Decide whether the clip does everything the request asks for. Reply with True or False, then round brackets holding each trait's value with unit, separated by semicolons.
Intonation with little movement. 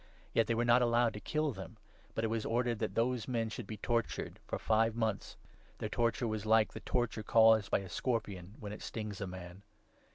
True (1.9 semitones)